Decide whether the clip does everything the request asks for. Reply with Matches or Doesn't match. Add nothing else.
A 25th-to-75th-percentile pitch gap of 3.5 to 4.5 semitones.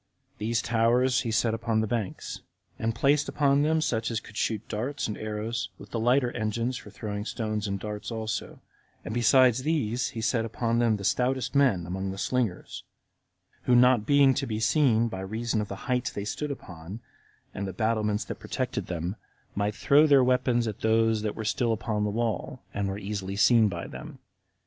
Doesn't match